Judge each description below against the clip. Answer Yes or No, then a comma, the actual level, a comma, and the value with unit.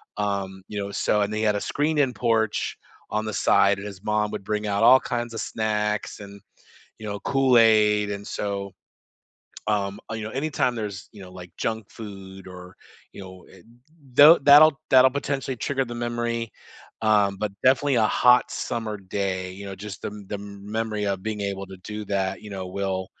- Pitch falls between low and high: No, low, 105 Hz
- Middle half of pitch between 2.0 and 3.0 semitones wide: Yes, average, 2.7 semitones